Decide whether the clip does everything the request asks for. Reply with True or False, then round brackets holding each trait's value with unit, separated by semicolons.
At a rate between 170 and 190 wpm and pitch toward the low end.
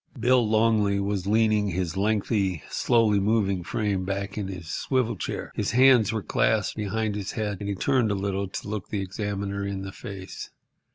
True (180 wpm; 100 Hz)